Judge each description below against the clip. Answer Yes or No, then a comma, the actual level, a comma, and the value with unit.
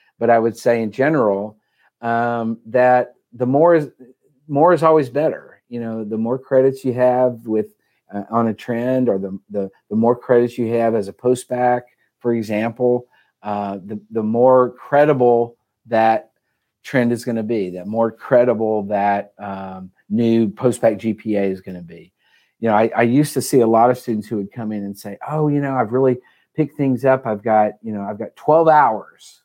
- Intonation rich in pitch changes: No, average, 2.7 semitones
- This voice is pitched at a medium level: No, low, 115 Hz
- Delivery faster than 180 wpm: Yes, average, 200 wpm